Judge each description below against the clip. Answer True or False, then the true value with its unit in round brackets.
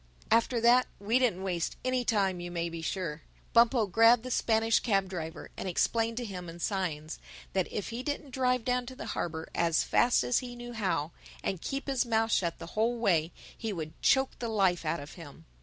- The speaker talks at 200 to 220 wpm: True (205 wpm)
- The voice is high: True (210 Hz)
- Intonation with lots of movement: True (5.9 semitones)